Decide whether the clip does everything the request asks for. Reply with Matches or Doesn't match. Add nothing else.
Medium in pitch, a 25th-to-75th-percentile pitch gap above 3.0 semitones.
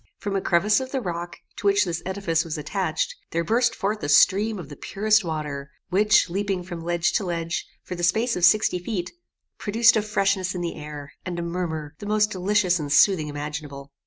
Matches